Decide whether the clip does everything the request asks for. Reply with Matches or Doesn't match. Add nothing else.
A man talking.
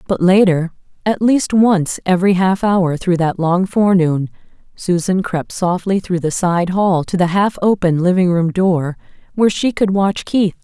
Doesn't match